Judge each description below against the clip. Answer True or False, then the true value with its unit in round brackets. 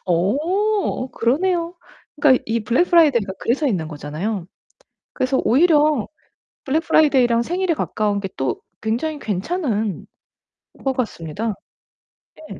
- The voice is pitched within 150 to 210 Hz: False (250 Hz)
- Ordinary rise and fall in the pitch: False (7.1 semitones)